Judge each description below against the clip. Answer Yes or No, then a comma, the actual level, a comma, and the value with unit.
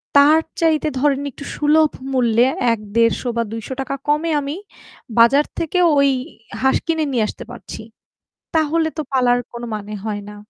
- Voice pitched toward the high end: Yes, very high, 275 Hz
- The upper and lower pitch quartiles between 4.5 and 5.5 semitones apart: Yes, average, 4.8 semitones